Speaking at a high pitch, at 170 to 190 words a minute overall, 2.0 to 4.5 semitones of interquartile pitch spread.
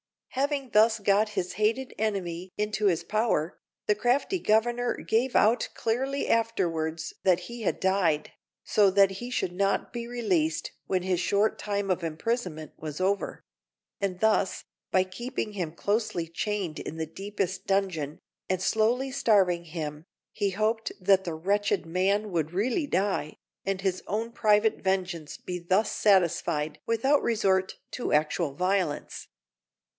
No: high, 195 Hz; average, 145 wpm; average, 3.8 semitones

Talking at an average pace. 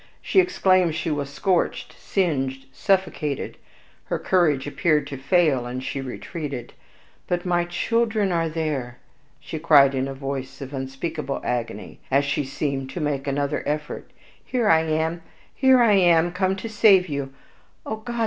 Yes: average, 155 wpm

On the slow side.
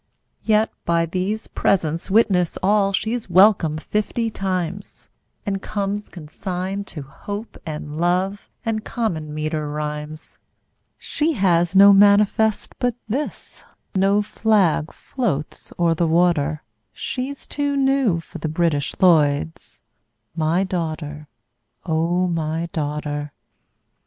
Yes: slow, 110 wpm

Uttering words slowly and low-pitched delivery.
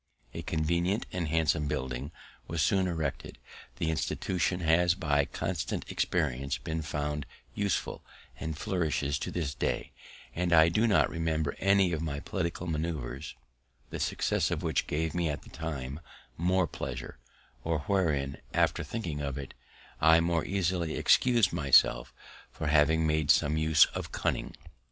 No: average, 145 wpm; very low, 80 Hz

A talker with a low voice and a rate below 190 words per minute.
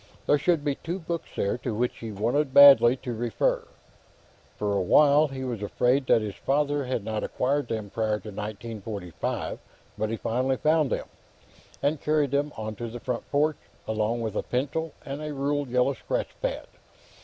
Yes: low, 125 Hz; average, 180 wpm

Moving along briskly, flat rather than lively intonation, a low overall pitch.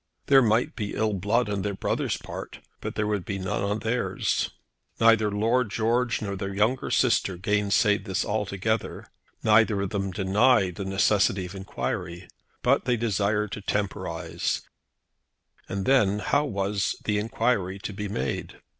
No: average, 155 wpm; narrow, 2.3 semitones; low, 105 Hz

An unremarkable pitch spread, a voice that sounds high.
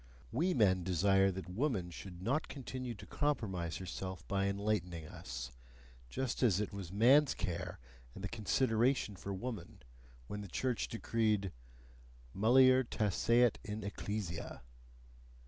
No: average, 4.4 semitones; low, 105 Hz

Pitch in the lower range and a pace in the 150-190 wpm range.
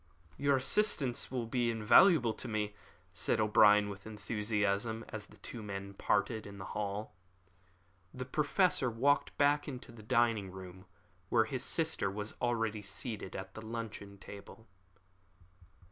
No: low, 110 Hz; average, 140 wpm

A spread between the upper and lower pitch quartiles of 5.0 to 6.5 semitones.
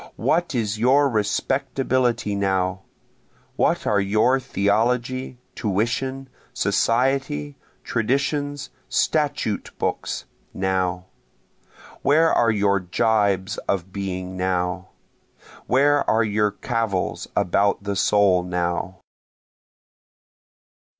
Yes: average, 5.3 semitones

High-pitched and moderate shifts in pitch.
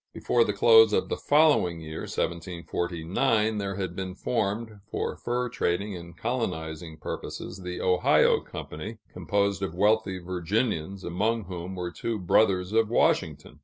No: very low, 95 Hz; average, 4.1 semitones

